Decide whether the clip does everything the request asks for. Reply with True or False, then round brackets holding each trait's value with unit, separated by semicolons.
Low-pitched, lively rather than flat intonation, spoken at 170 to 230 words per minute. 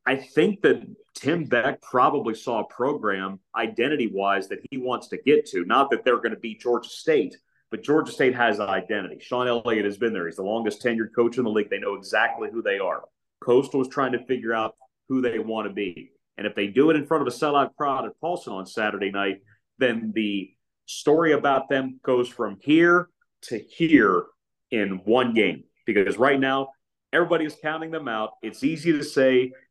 True (130 Hz; 6.0 semitones; 205 wpm)